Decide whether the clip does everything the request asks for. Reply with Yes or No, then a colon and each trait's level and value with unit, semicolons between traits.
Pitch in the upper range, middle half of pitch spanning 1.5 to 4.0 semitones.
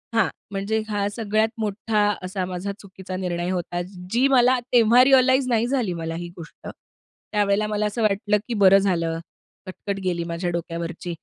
Yes: high, 200 Hz; average, 3.7 semitones